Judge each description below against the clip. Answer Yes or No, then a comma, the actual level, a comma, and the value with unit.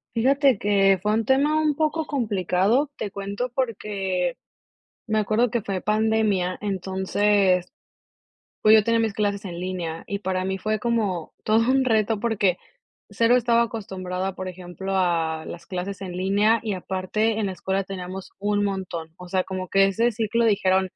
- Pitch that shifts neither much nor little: Yes, average, 3.1 semitones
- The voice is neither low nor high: No, high, 200 Hz